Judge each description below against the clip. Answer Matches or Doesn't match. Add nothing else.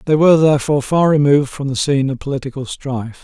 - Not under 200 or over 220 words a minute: Matches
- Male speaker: Matches